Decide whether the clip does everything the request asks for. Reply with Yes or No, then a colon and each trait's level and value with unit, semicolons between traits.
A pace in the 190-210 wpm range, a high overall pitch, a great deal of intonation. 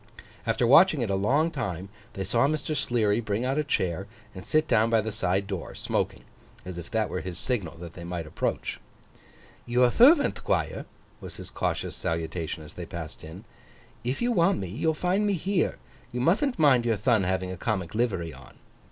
No: average, 195 wpm; low, 110 Hz; wide, 7.7 semitones